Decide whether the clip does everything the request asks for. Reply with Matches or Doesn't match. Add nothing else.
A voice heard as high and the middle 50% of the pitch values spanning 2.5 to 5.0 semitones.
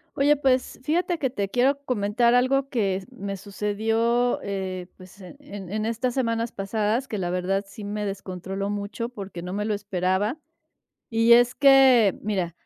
Matches